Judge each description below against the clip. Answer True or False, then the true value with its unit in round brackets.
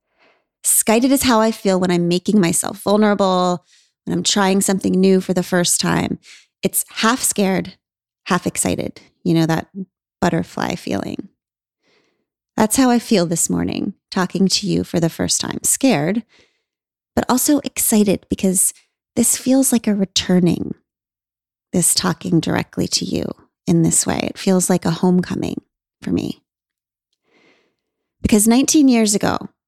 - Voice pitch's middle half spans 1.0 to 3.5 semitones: False (3.9 semitones)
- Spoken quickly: False (145 wpm)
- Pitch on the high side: True (195 Hz)